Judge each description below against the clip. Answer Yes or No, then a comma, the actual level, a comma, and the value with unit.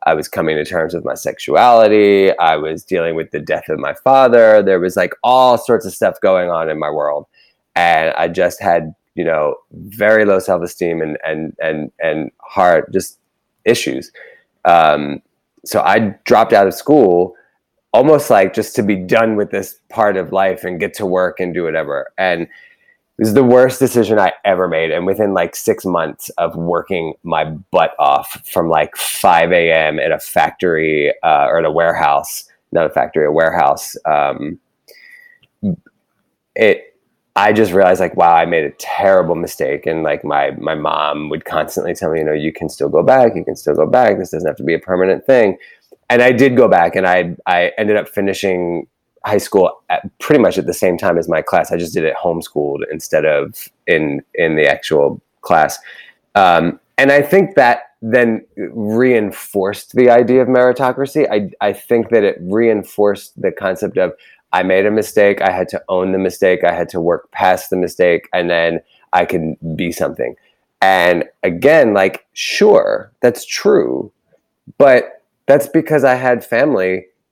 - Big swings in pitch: Yes, wide, 7.1 semitones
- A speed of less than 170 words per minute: No, average, 185 wpm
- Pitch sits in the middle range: No, low, 100 Hz